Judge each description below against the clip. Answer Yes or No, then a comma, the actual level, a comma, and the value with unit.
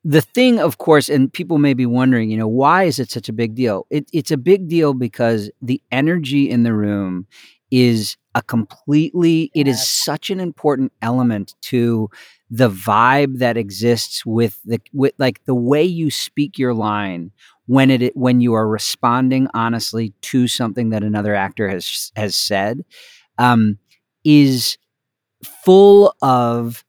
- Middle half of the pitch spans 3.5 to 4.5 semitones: Yes, average, 4.1 semitones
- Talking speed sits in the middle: Yes, average, 160 wpm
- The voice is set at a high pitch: No, low, 125 Hz